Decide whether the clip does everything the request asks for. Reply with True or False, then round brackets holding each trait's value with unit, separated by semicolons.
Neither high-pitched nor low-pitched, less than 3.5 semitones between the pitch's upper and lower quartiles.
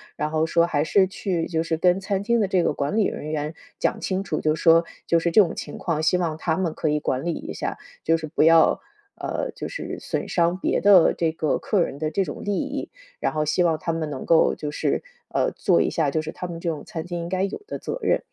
True (165 Hz; 2.9 semitones)